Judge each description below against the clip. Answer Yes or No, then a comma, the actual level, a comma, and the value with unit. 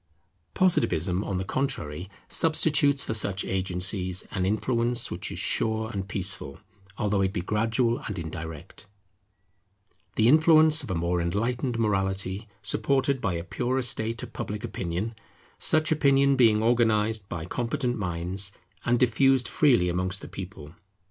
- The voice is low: Yes, low, 105 Hz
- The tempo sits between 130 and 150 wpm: Yes, average, 140 wpm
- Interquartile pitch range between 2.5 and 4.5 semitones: No, average, 5.0 semitones